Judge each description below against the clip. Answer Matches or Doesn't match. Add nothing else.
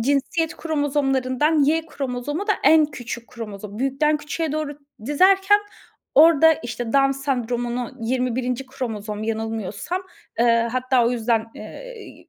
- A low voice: Doesn't match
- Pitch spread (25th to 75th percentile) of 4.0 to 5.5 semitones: Matches